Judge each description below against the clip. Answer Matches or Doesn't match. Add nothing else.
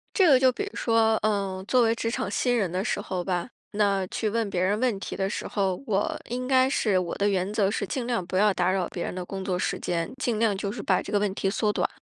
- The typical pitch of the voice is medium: Doesn't match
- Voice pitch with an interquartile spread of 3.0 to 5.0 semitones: Matches